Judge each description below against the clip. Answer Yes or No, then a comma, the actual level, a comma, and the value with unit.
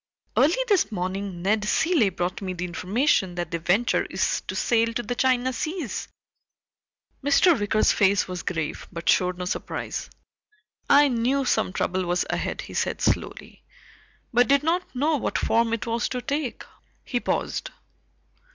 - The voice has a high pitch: Yes, high, 230 Hz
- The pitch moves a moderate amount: No, wide, 6.7 semitones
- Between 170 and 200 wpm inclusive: No, average, 160 wpm